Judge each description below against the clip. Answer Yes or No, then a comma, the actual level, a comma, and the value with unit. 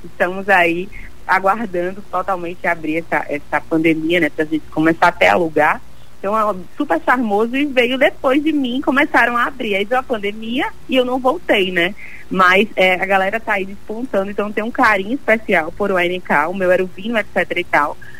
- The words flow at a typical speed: No, fast, 190 wpm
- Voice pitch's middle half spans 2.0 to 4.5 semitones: No, average, 5.3 semitones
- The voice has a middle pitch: No, high, 195 Hz